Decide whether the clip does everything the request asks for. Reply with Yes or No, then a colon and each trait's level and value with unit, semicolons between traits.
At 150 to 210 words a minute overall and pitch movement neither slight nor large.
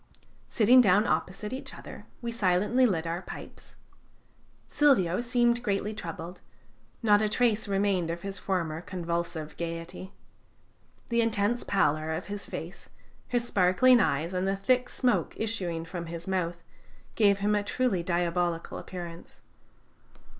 No: slow, 135 wpm; average, 4.4 semitones